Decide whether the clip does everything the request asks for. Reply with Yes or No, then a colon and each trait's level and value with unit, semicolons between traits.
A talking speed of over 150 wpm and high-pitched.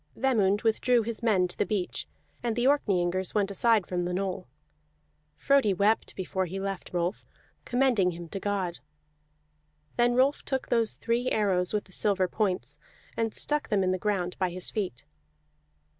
Yes: average, 160 wpm; high, 200 Hz